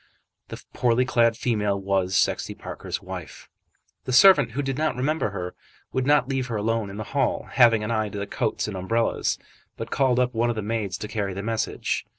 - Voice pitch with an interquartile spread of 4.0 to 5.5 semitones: No, average, 3.6 semitones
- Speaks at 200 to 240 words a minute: Yes, fast, 205 wpm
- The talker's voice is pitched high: No, low, 115 Hz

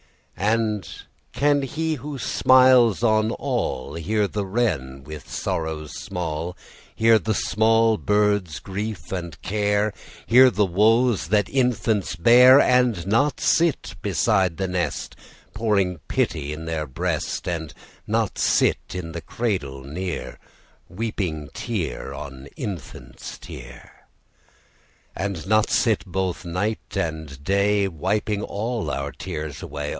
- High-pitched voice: No, low, 100 Hz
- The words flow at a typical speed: No, slow, 120 wpm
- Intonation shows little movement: No, wide, 5.5 semitones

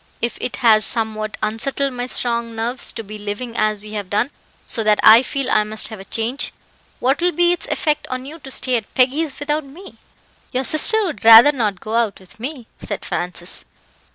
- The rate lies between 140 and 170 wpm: No, fast, 205 wpm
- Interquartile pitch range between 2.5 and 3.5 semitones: No, average, 4.2 semitones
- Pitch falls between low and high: No, high, 235 Hz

